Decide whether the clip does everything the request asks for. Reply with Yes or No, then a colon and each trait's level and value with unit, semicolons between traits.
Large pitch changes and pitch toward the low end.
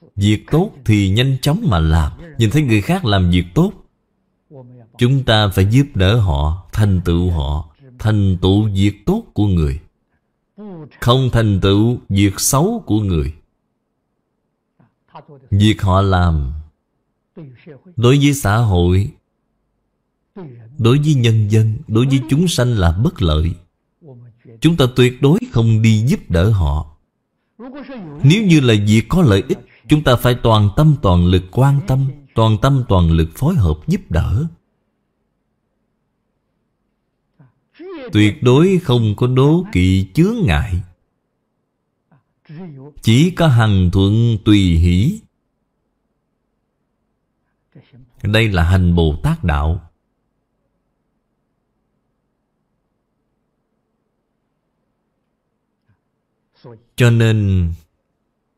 Yes: wide, 6.9 semitones; low, 115 Hz